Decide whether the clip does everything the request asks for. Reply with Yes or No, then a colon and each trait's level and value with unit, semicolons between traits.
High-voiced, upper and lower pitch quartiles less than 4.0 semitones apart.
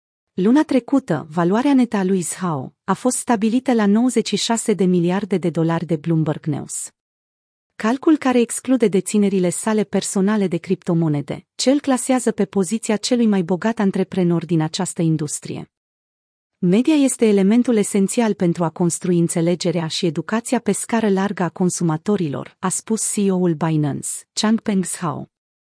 No: high, 195 Hz; average, 4.7 semitones